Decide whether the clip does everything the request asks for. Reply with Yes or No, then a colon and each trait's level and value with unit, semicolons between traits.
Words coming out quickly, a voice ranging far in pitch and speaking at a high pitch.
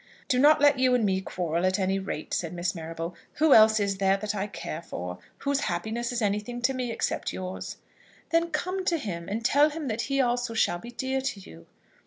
Yes: fast, 220 wpm; wide, 5.9 semitones; high, 220 Hz